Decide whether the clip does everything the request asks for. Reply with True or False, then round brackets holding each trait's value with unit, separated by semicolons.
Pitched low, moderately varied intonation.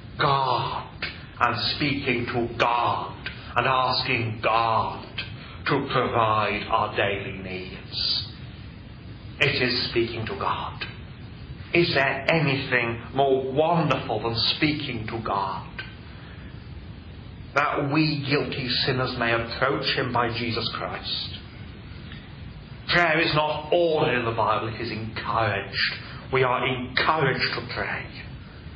True (120 Hz; 3.4 semitones)